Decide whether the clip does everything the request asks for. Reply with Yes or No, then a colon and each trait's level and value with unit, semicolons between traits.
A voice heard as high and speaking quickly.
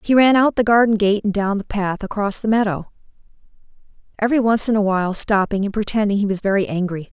Yes: high, 205 Hz; fast, 210 wpm